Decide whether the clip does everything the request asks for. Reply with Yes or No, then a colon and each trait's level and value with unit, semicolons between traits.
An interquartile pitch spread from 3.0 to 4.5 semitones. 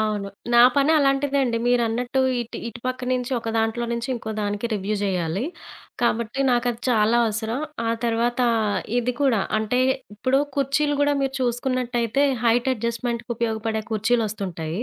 No: narrow, 2.4 semitones